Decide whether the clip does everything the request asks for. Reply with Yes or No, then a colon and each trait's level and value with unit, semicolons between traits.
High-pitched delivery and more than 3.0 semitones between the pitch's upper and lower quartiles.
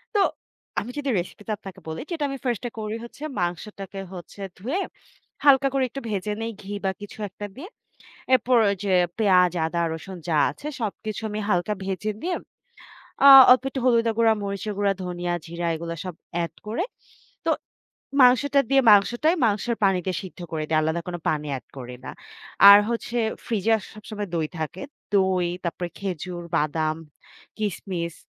Yes: high, 200 Hz; average, 4.7 semitones